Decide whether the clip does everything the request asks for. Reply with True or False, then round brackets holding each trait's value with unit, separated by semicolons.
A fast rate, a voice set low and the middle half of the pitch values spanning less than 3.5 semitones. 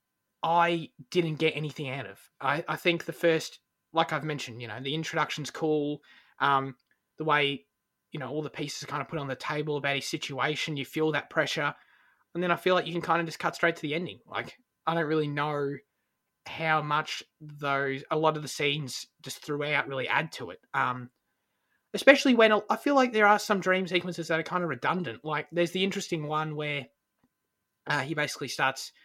False (210 wpm; 155 Hz; 3.0 semitones)